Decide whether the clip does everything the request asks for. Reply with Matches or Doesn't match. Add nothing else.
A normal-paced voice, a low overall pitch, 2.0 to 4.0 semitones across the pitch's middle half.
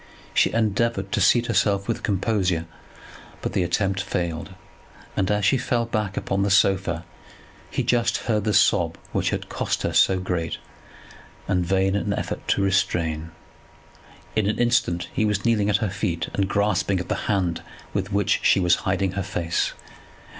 Matches